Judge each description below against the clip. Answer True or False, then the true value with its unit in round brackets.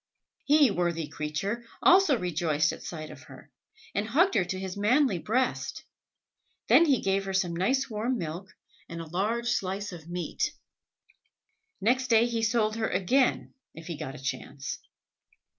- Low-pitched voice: False (195 Hz)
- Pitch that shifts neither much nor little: False (5.8 semitones)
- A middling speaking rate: True (160 wpm)